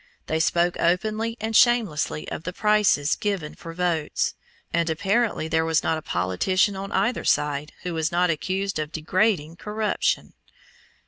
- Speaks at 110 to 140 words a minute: No, average, 150 wpm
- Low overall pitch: No, medium, 175 Hz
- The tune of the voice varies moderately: Yes, average, 4.6 semitones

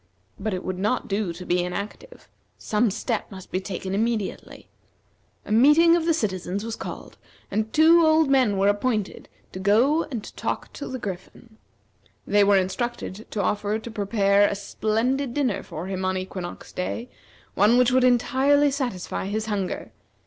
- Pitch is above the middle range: Yes, high, 215 Hz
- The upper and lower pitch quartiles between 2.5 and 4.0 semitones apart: No, average, 4.6 semitones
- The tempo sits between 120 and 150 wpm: No, average, 165 wpm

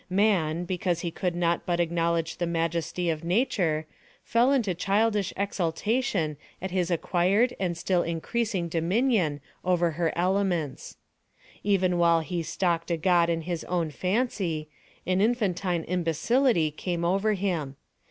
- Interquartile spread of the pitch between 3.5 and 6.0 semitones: No, average, 2.8 semitones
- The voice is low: No, medium, 175 Hz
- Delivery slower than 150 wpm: Yes, slow, 135 wpm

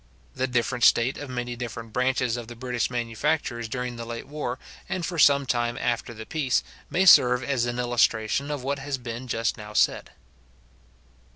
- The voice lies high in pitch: No, low, 125 Hz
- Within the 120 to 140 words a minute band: No, average, 180 wpm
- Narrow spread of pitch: Yes, narrow, 2.3 semitones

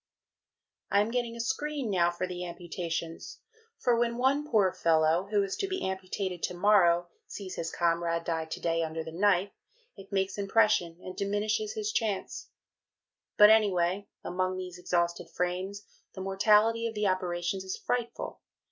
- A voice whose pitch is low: No, high, 190 Hz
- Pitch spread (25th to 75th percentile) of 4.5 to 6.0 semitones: No, average, 3.5 semitones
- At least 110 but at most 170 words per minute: Yes, average, 160 wpm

